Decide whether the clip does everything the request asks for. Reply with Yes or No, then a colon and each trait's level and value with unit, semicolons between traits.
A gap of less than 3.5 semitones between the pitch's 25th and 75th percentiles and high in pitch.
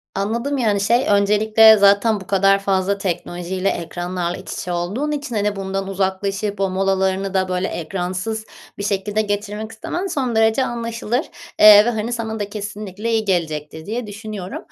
Yes: narrow, 2.6 semitones; high, 205 Hz